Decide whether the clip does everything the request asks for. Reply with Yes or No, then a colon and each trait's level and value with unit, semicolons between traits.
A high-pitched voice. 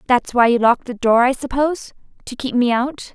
Yes: very high, 250 Hz